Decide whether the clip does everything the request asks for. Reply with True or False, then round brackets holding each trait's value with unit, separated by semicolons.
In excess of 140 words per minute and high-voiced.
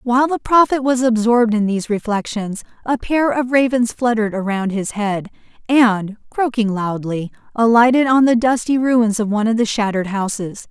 True (170 wpm; 230 Hz)